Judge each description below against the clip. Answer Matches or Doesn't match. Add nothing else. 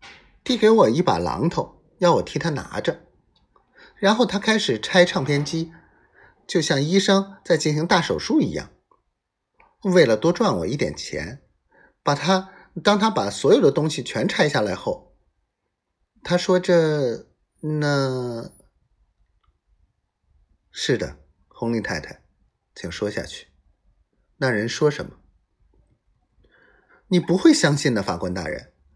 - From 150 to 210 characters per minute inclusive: Matches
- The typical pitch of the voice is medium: Matches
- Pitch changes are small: Doesn't match